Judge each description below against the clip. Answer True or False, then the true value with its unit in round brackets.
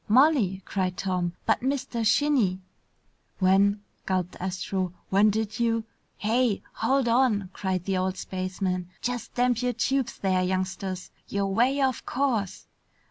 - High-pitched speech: True (200 Hz)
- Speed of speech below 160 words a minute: True (145 wpm)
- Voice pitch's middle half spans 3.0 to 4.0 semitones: False (4.6 semitones)